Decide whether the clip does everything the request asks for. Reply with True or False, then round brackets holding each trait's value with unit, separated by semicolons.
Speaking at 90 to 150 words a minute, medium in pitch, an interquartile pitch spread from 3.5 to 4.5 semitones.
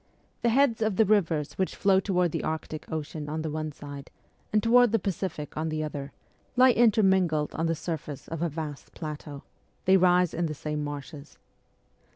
False (185 wpm; 160 Hz; 4.2 semitones)